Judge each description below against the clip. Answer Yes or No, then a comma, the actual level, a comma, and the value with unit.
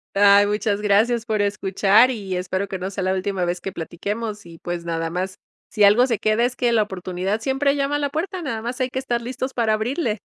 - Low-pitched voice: No, high, 210 Hz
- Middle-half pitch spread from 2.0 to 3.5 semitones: No, average, 4.2 semitones